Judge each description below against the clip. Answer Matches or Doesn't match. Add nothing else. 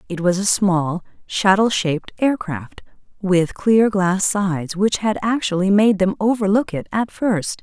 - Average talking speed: Matches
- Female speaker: Matches